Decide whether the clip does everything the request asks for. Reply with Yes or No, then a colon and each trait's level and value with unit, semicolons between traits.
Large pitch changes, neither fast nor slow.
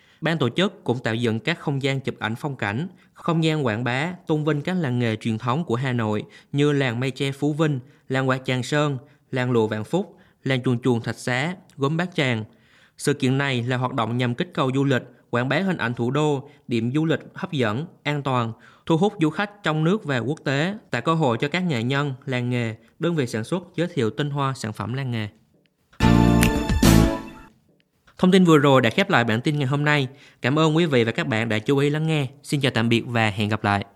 No: average, 4.7 semitones; average, 240 wpm